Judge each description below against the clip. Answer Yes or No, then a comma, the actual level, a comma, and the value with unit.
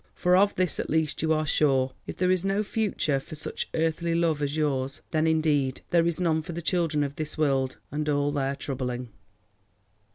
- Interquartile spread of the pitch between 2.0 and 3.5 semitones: Yes, average, 3.1 semitones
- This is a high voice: No, medium, 155 Hz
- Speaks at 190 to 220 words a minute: Yes, average, 200 wpm